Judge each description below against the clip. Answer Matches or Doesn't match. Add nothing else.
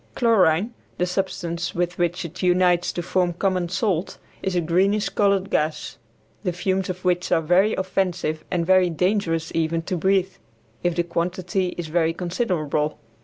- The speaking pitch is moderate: Matches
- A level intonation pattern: Matches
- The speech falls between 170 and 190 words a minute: Doesn't match